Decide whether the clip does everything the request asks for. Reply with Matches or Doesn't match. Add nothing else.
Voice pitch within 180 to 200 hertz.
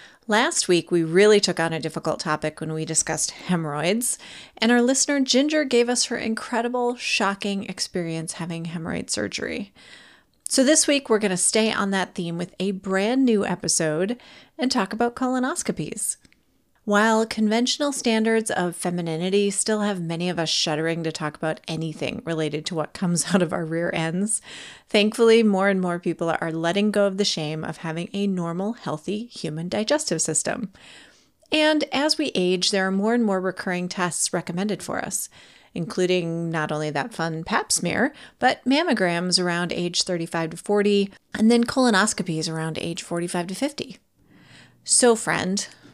Matches